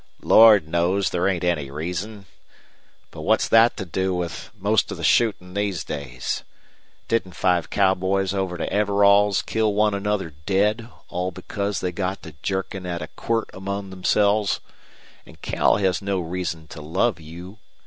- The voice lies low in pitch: Yes, very low, 95 Hz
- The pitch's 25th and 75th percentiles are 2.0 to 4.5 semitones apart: Yes, narrow, 2.4 semitones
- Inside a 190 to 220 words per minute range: No, average, 160 wpm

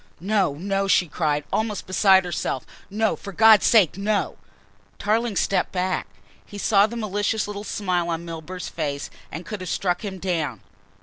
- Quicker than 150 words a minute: Yes, average, 165 wpm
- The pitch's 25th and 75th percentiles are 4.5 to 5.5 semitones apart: No, average, 3.2 semitones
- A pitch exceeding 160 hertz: Yes, high, 190 Hz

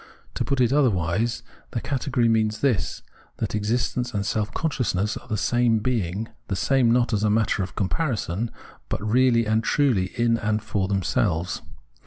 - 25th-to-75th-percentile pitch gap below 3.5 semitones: Yes, average, 3.0 semitones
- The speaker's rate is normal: Yes, average, 170 wpm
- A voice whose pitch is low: Yes, low, 110 Hz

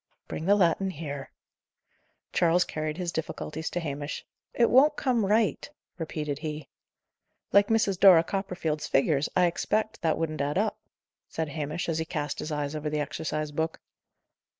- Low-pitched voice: No, medium, 160 Hz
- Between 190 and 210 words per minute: No, average, 155 wpm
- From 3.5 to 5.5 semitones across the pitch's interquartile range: Yes, average, 4.0 semitones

